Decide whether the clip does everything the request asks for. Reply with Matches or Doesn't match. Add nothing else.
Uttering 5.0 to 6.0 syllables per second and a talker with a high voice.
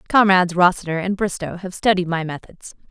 Doesn't match